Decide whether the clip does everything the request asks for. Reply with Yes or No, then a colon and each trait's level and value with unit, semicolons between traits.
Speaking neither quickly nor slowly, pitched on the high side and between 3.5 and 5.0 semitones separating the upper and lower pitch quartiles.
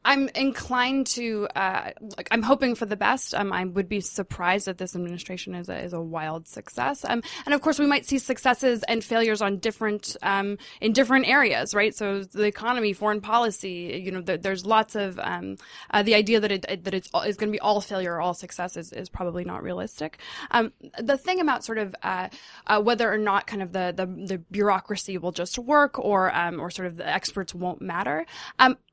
No: fast, 215 wpm; high, 205 Hz; average, 4.2 semitones